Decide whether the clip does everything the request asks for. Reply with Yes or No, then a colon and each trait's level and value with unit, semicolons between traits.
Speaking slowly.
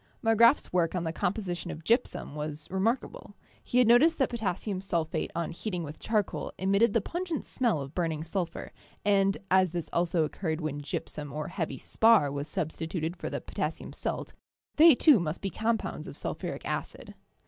No: average, 180 wpm